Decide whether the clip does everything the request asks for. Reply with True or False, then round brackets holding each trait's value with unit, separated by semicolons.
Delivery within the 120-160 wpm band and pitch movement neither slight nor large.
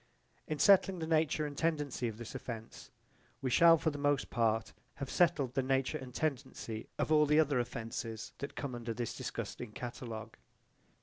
False (175 wpm; 4.4 semitones)